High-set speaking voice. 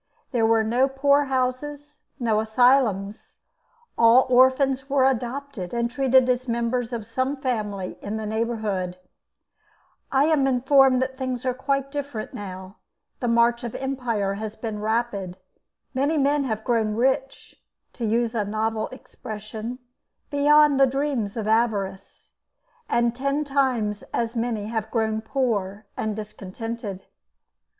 Yes: high, 235 Hz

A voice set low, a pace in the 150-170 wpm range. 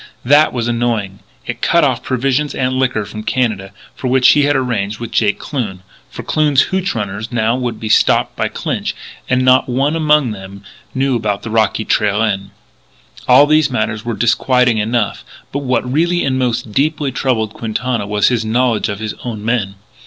No: low, 120 Hz; average, 180 wpm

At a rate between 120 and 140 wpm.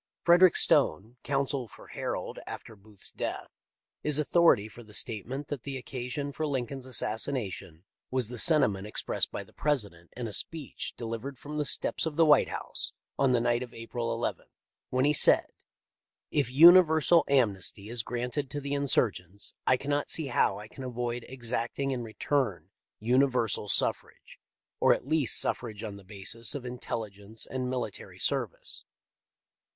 No: average, 160 wpm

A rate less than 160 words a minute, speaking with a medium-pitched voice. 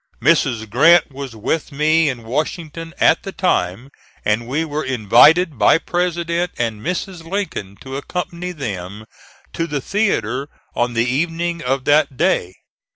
Yes: average, 145 wpm; medium, 145 Hz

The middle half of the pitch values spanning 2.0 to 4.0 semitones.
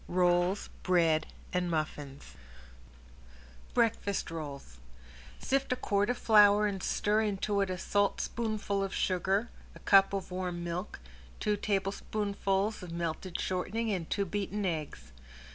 Yes: average, 2.8 semitones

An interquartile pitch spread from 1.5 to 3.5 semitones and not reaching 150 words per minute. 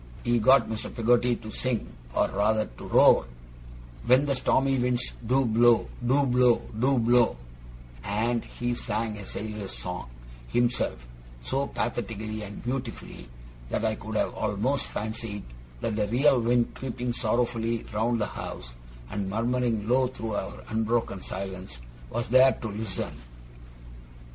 Yes: narrow, 2.5 semitones; average, 140 wpm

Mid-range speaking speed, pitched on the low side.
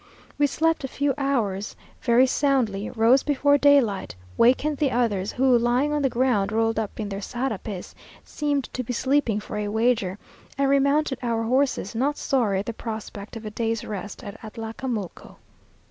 No: average, 170 wpm; high, 240 Hz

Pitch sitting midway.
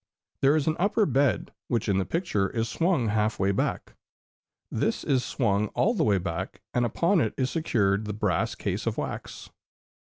No: low, 115 Hz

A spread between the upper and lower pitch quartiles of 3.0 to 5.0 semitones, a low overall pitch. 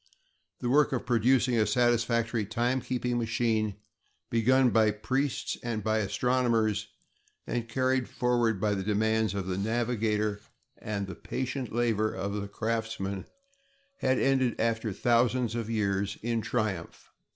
No: narrow, 2.5 semitones; low, 115 Hz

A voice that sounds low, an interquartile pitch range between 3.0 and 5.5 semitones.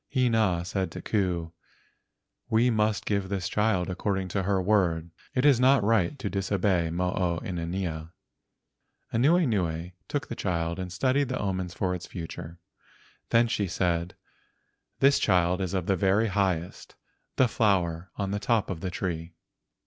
Yes: very low, 95 Hz; average, 3.5 semitones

